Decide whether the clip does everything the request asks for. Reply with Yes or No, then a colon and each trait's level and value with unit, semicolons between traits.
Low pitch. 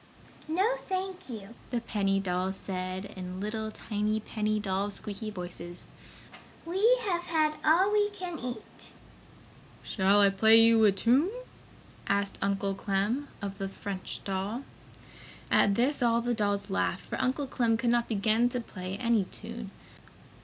No: high, 215 Hz